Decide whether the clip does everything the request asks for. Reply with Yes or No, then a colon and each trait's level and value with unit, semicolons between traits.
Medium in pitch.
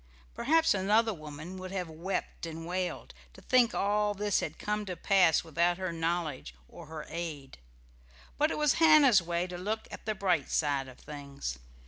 Yes: medium, 180 Hz